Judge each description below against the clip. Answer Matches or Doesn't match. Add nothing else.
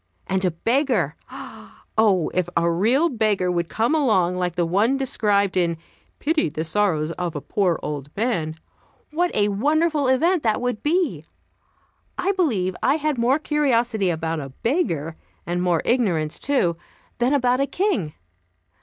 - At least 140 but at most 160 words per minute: Matches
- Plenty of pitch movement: Matches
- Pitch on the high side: Matches